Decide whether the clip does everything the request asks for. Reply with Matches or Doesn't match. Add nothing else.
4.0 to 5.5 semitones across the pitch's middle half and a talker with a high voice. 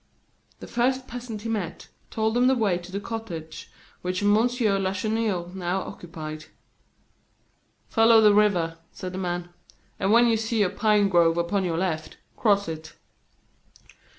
Matches